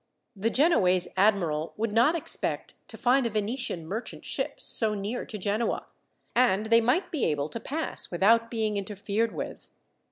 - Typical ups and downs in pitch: Yes, average, 3.2 semitones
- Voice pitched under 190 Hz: No, high, 220 Hz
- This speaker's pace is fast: No, average, 160 wpm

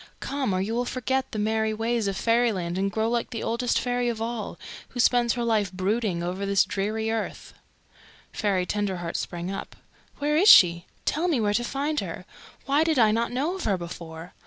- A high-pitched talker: Yes, high, 220 Hz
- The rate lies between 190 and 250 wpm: Yes, average, 200 wpm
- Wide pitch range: No, average, 3.9 semitones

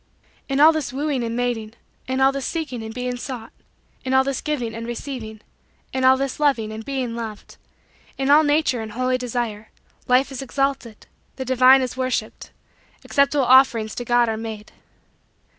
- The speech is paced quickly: No, average, 175 wpm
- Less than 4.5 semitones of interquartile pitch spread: Yes, average, 2.8 semitones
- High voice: Yes, very high, 255 Hz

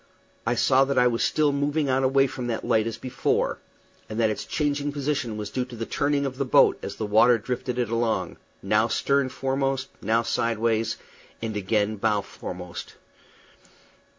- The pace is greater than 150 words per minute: Yes, average, 180 wpm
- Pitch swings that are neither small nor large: Yes, average, 3.6 semitones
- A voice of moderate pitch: No, low, 120 Hz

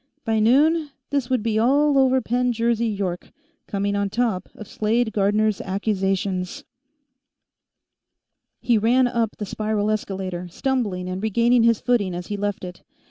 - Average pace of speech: Yes, average, 145 wpm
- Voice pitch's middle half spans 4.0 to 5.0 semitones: No, average, 3.6 semitones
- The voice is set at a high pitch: Yes, high, 215 Hz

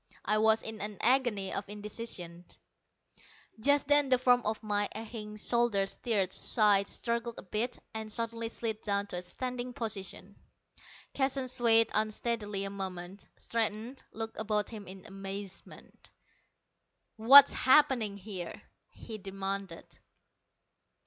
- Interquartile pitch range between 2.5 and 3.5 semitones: Yes, average, 2.9 semitones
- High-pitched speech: Yes, high, 215 Hz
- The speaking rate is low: Yes, slow, 125 wpm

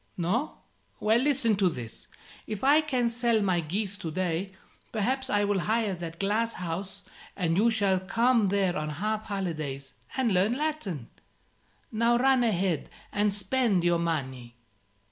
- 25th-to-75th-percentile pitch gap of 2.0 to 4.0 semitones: No, average, 4.9 semitones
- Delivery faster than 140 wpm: Yes, average, 150 wpm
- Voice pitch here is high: Yes, high, 200 Hz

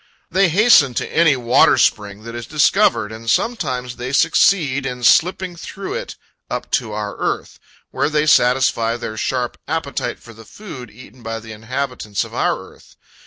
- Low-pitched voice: Yes, low, 125 Hz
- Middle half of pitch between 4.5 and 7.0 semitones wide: Yes, average, 5.3 semitones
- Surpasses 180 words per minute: No, average, 165 wpm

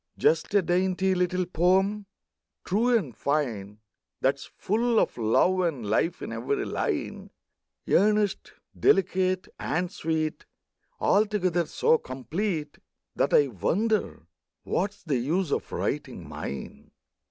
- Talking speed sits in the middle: No, slow, 120 wpm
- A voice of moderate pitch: Yes, medium, 180 Hz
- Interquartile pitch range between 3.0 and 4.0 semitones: No, average, 5.3 semitones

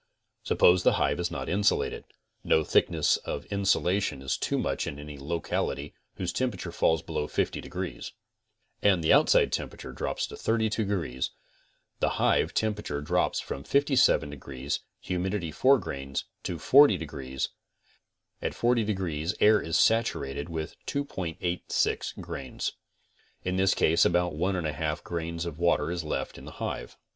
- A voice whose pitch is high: No, very low, 85 Hz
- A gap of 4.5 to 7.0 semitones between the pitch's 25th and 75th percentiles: Yes, average, 5.0 semitones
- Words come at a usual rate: Yes, average, 150 wpm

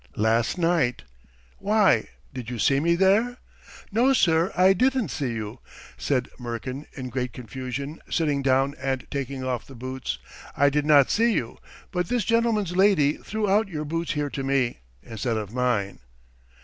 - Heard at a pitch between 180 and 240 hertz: No, medium, 140 Hz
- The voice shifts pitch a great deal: Yes, wide, 6.9 semitones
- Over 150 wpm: Yes, average, 160 wpm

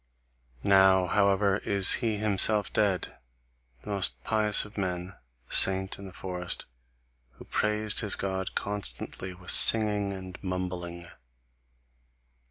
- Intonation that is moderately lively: No, narrow, 2.0 semitones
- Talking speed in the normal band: No, slow, 120 wpm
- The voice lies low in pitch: Yes, very low, 95 Hz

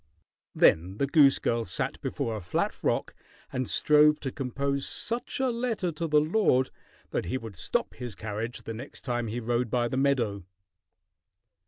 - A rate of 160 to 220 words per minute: Yes, average, 170 wpm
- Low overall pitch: Yes, low, 130 Hz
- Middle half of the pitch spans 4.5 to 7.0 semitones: Yes, average, 4.8 semitones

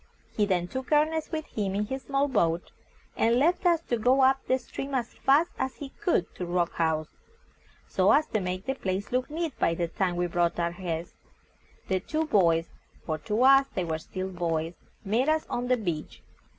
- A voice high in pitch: Yes, high, 210 Hz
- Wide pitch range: Yes, wide, 7.6 semitones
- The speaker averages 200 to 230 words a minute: Yes, fast, 205 wpm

